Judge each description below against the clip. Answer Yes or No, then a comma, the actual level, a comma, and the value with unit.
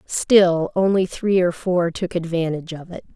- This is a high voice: No, medium, 175 Hz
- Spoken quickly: No, average, 170 wpm